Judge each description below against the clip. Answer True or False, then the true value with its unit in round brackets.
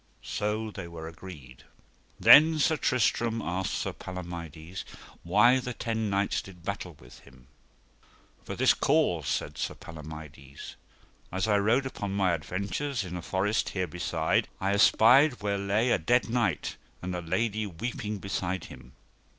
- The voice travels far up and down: False (4.6 semitones)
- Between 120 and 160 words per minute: True (150 wpm)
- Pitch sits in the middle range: False (100 Hz)